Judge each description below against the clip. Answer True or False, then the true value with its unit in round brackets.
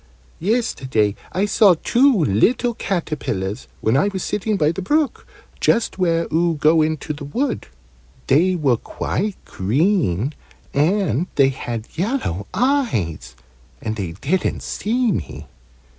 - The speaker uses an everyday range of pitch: False (8.3 semitones)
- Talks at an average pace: False (130 wpm)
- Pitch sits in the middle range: True (165 Hz)